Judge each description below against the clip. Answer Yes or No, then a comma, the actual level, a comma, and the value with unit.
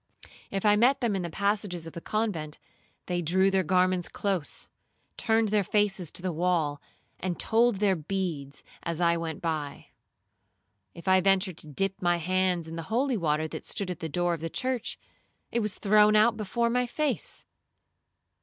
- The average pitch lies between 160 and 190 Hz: Yes, medium, 185 Hz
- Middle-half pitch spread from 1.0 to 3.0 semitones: No, average, 3.9 semitones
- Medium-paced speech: Yes, average, 180 wpm